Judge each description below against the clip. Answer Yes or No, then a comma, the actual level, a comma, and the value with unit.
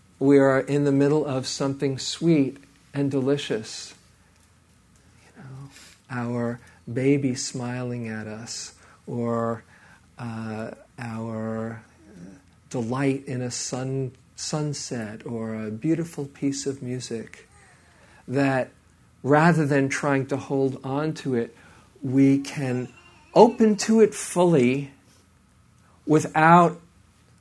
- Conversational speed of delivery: No, slow, 105 wpm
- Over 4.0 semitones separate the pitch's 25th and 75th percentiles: No, average, 3.6 semitones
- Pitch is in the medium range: No, low, 130 Hz